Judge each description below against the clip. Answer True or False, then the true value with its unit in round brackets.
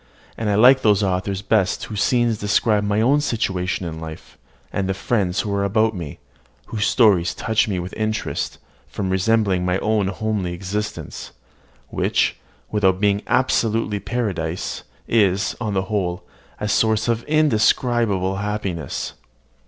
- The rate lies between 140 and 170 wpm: True (145 wpm)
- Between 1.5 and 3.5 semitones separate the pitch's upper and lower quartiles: True (2.8 semitones)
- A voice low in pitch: True (105 Hz)